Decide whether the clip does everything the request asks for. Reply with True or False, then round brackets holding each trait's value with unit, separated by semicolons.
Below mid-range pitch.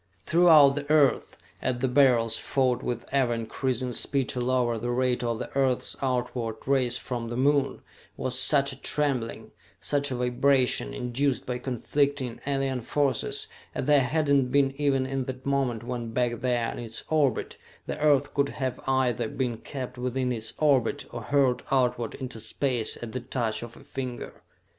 True (130 Hz)